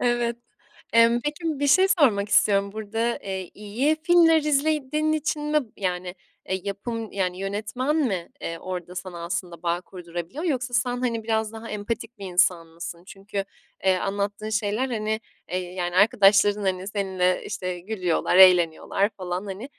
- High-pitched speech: Yes, high, 205 Hz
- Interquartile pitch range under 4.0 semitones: No, average, 4.7 semitones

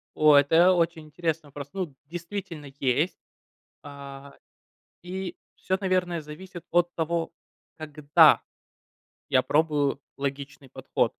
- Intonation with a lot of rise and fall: No, average, 3.5 semitones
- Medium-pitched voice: Yes, medium, 160 Hz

